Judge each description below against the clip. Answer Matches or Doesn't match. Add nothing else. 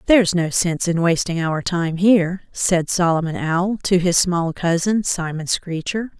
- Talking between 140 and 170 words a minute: Matches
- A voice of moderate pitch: Matches